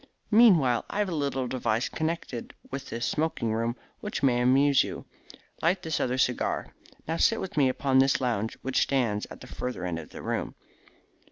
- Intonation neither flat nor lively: Yes, average, 4.8 semitones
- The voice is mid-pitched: No, low, 130 Hz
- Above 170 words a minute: Yes, average, 185 wpm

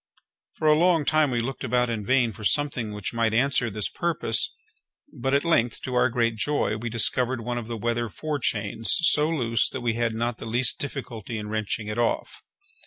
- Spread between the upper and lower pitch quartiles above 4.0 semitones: No, average, 3.1 semitones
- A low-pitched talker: Yes, low, 120 Hz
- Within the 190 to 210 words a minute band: Yes, average, 200 wpm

